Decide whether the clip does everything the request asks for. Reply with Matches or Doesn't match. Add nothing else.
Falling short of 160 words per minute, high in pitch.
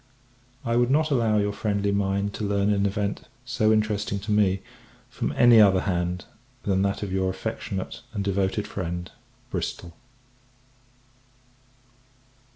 Doesn't match